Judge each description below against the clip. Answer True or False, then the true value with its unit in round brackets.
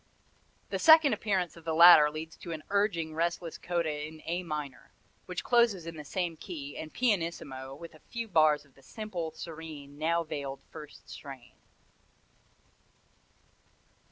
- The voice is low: False (160 Hz)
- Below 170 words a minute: True (150 wpm)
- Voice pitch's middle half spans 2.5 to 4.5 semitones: True (2.8 semitones)